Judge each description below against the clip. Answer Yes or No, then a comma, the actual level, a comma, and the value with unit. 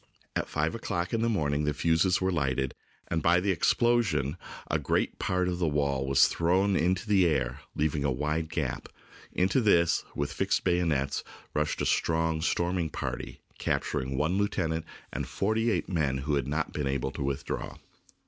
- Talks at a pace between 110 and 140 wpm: No, average, 175 wpm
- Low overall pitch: Yes, very low, 80 Hz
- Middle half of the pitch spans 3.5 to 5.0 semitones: Yes, average, 4.2 semitones